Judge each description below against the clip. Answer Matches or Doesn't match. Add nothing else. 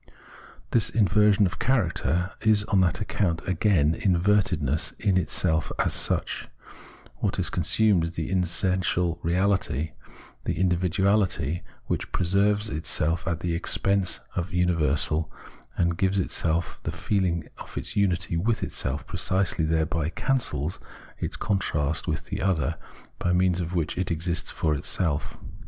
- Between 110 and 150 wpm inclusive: Matches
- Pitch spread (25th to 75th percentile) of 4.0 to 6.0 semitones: Doesn't match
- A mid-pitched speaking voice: Doesn't match